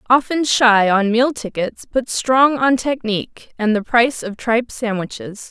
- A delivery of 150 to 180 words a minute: Yes, average, 165 wpm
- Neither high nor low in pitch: No, high, 235 Hz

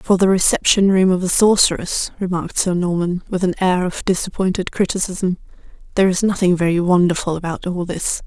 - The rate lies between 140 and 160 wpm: No, average, 175 wpm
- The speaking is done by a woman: Yes, female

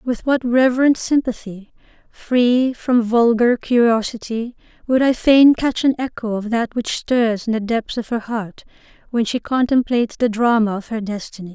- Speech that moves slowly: No, average, 165 wpm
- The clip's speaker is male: No, female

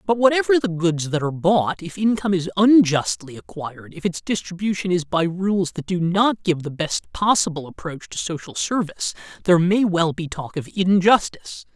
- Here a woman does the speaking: No, male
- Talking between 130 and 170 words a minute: No, average, 185 wpm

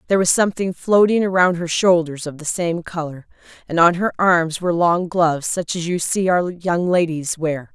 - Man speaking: No, female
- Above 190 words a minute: Yes, average, 200 wpm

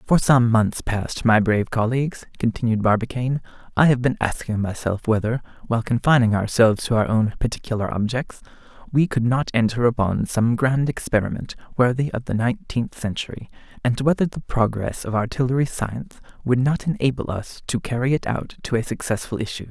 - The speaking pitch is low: Yes, low, 120 Hz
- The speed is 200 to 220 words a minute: No, average, 165 wpm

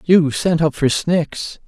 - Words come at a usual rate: Yes, average, 180 wpm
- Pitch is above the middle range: No, medium, 155 Hz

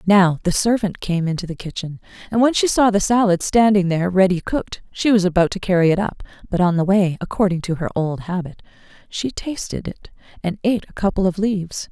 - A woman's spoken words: Yes, female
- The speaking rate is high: Yes, fast, 210 wpm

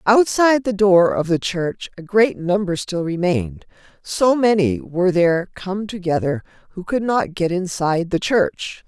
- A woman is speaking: Yes, female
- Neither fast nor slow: Yes, average, 160 wpm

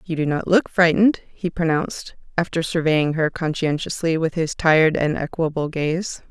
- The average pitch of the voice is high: No, medium, 165 Hz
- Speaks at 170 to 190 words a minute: No, average, 160 wpm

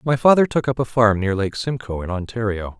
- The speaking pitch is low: Yes, low, 115 Hz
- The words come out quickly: Yes, fast, 235 wpm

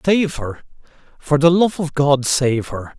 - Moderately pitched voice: Yes, medium, 145 Hz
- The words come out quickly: No, average, 180 wpm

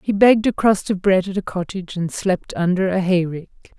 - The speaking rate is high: Yes, fast, 220 wpm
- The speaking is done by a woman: Yes, female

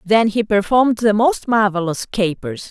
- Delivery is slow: No, average, 155 wpm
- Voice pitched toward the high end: Yes, high, 210 Hz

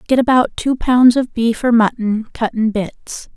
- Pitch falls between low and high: No, high, 235 Hz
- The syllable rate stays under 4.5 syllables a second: Yes, 4.2 syllables/s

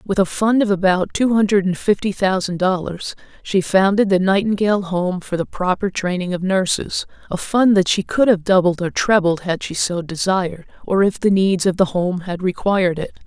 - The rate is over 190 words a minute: Yes, average, 200 wpm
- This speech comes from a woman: Yes, female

